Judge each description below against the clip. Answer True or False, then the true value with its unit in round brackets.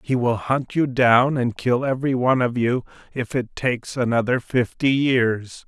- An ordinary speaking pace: True (180 wpm)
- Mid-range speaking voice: False (125 Hz)